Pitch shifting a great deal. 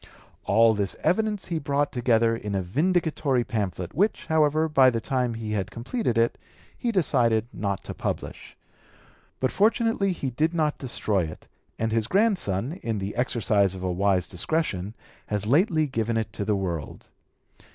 Yes: wide, 7.3 semitones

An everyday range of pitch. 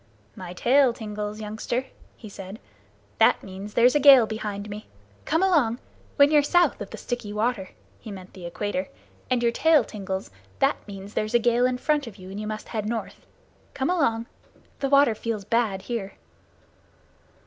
Yes: average, 3.6 semitones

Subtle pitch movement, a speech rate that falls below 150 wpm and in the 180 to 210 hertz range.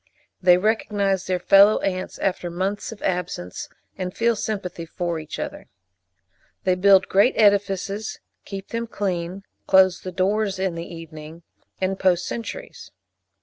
Yes: narrow, 2.2 semitones; average, 140 wpm; high, 190 Hz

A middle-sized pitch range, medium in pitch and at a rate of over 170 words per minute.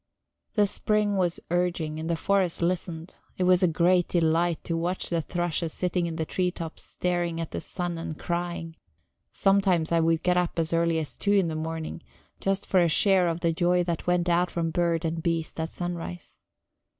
No: narrow, 1.5 semitones; medium, 170 Hz; average, 200 wpm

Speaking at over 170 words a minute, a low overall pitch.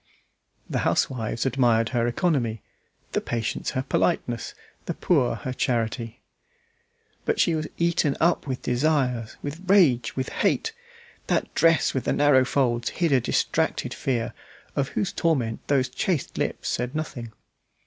No: average, 140 wpm; low, 130 Hz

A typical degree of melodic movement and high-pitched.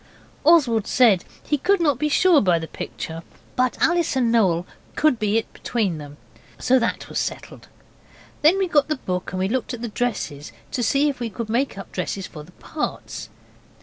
No: wide, 7.4 semitones; high, 235 Hz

